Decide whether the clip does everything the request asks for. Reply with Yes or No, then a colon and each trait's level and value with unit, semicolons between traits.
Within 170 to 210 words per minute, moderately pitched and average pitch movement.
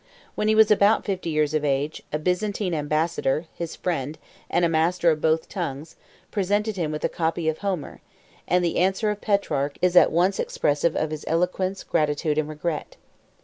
Yes: average, 185 wpm; medium, 165 Hz; average, 3.5 semitones